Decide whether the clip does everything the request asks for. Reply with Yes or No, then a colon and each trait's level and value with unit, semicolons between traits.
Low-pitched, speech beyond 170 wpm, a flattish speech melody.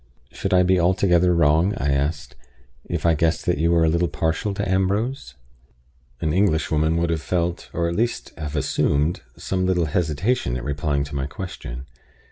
No: very low, 85 Hz; average, 180 wpm; average, 3.7 semitones